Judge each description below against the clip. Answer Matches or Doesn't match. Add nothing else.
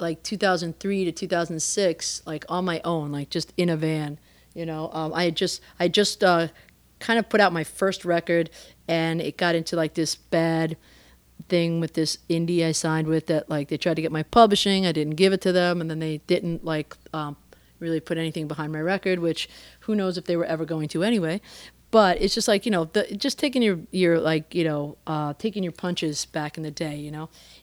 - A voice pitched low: Doesn't match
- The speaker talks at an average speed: Doesn't match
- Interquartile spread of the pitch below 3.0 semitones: Matches